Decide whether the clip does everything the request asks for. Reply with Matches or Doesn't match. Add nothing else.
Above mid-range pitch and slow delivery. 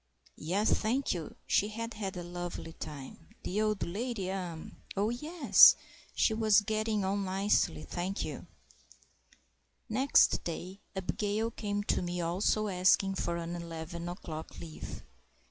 Matches